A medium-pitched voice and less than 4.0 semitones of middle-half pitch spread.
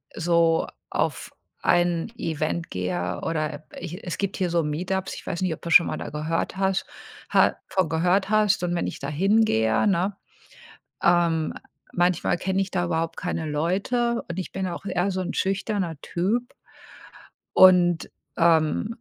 Yes: medium, 175 Hz; average, 2.8 semitones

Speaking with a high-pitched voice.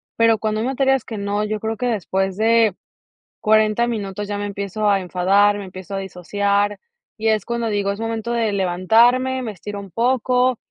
Yes: high, 210 Hz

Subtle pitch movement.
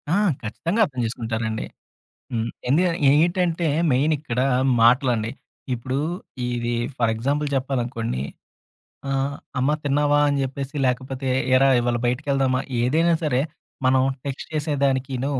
No: average, 3.1 semitones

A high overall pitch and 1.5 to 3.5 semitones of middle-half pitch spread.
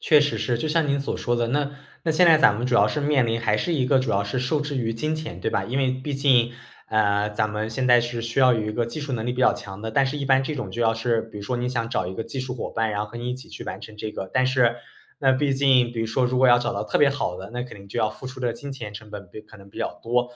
No: low, 120 Hz; average, 3.2 semitones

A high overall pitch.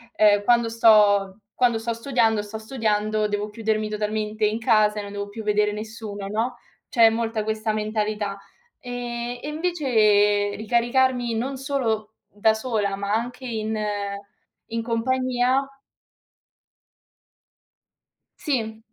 Yes: high, 220 Hz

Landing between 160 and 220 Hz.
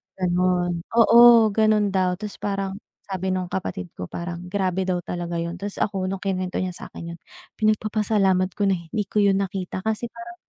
Yes: high, 190 Hz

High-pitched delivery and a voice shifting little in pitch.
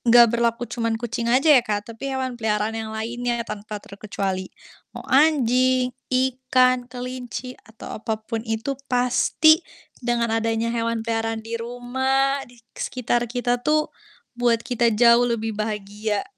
Yes: high, 235 Hz; narrow, 2.1 semitones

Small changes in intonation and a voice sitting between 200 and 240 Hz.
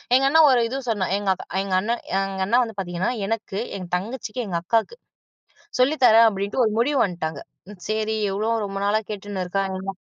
No: average, 3.3 semitones; high, 205 Hz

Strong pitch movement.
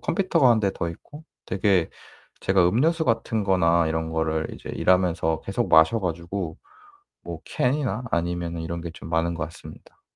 No: average, 5.0 semitones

